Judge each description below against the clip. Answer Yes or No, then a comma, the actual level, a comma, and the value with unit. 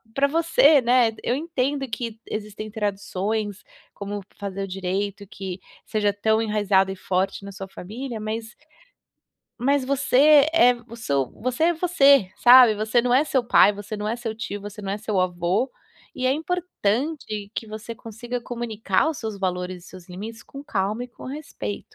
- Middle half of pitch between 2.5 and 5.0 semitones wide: Yes, average, 4.2 semitones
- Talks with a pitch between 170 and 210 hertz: No, high, 220 Hz